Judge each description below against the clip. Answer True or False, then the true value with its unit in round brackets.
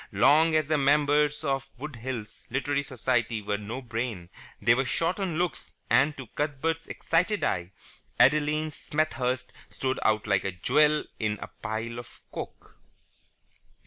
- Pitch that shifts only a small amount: False (4.7 semitones)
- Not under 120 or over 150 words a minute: True (145 wpm)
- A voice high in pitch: False (135 Hz)